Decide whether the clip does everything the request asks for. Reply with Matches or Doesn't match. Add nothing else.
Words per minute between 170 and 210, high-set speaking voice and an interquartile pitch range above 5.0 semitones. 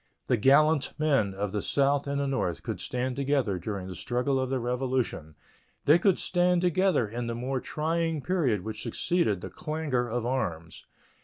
Doesn't match